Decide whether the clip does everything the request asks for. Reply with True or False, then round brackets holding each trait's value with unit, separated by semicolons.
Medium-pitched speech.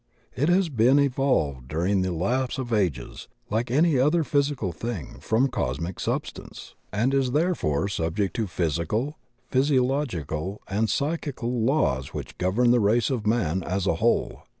False (115 Hz)